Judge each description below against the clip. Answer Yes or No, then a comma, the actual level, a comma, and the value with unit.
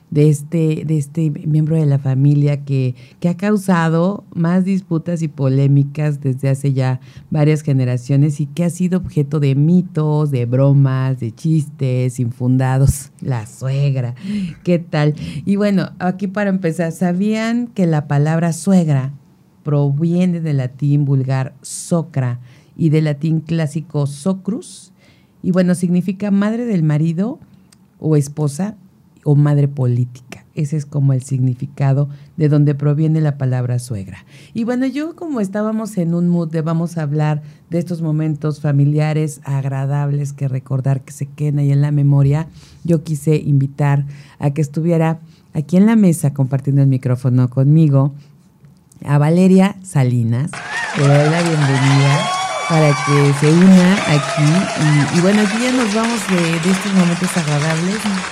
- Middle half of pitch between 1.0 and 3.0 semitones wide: No, average, 3.7 semitones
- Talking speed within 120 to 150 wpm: Yes, average, 145 wpm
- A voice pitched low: No, medium, 150 Hz